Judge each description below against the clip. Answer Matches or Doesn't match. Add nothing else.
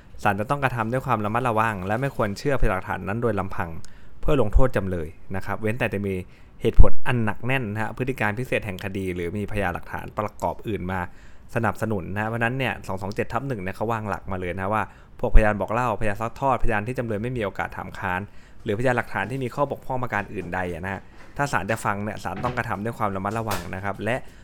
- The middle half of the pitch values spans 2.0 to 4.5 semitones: Matches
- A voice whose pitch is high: Doesn't match